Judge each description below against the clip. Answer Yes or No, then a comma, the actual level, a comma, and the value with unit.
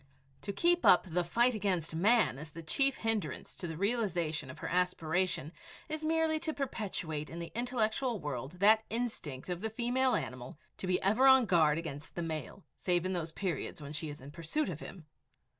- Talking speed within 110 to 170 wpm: No, average, 190 wpm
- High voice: No, medium, 180 Hz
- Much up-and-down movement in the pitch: Yes, wide, 6.5 semitones